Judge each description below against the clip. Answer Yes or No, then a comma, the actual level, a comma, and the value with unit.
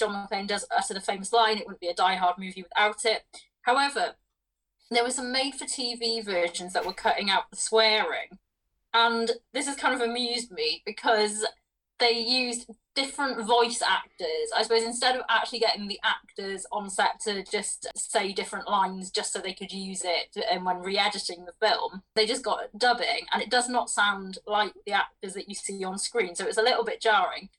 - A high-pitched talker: Yes, high, 220 Hz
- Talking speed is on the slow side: No, average, 195 wpm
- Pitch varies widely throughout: No, average, 3.3 semitones